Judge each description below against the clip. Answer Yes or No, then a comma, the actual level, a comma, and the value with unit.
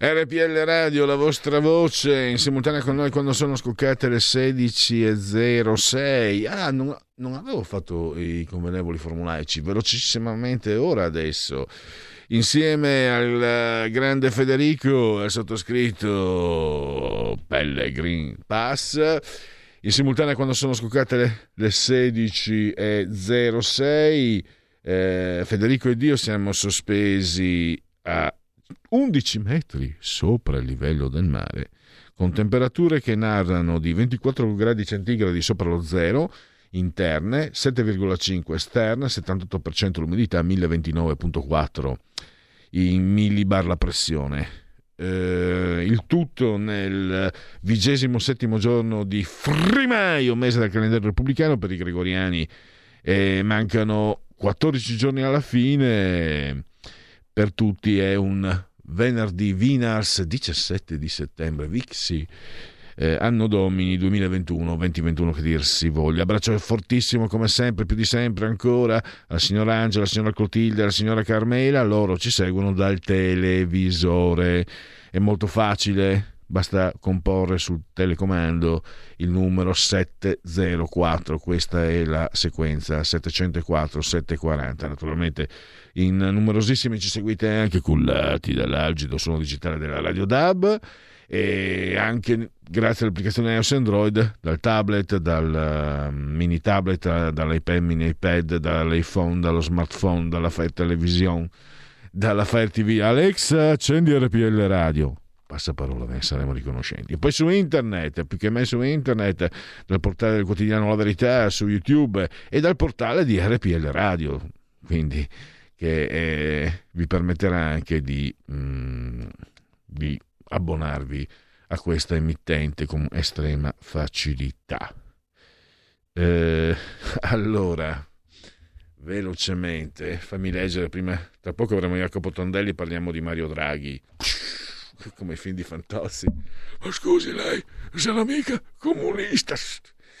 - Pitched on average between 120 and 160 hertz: No, very low, 95 Hz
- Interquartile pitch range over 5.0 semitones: Yes, wide, 5.4 semitones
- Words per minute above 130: No, slow, 115 wpm